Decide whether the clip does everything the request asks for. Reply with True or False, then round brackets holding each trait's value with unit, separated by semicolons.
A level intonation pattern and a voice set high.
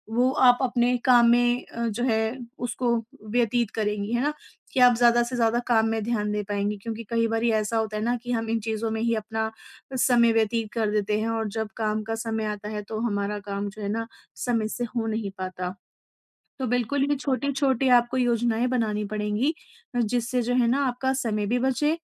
True (2.2 semitones; 230 Hz)